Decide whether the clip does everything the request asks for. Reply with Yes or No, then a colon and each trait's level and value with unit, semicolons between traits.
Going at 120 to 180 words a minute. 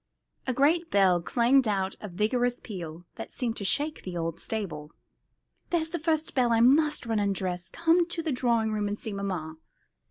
No: average, 195 wpm